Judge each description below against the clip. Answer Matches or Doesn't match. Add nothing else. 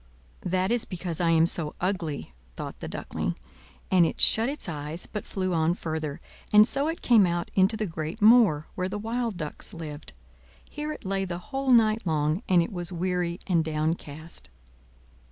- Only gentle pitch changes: Doesn't match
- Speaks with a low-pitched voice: Doesn't match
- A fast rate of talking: Doesn't match